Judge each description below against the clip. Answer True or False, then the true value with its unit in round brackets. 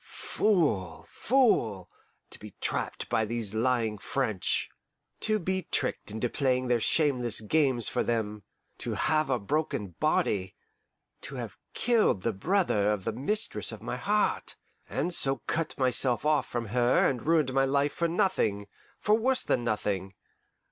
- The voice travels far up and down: True (6.7 semitones)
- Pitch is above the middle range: False (125 Hz)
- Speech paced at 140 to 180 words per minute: True (150 wpm)